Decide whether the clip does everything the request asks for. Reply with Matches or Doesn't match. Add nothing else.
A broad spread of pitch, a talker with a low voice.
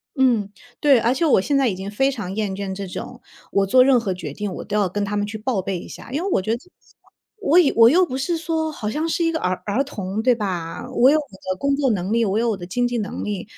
Doesn't match